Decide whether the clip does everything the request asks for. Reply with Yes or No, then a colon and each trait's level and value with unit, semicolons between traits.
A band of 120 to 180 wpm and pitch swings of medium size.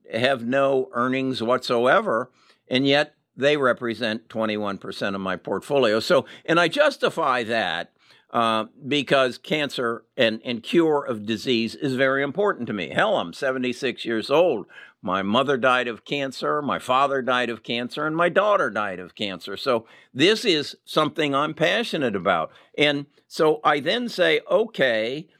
Yes: average, 150 wpm; average, 3.9 semitones